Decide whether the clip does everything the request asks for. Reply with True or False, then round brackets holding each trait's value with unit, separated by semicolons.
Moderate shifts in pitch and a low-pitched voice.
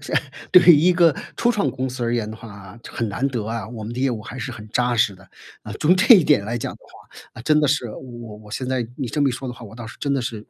True (3.9 semitones; 120 Hz)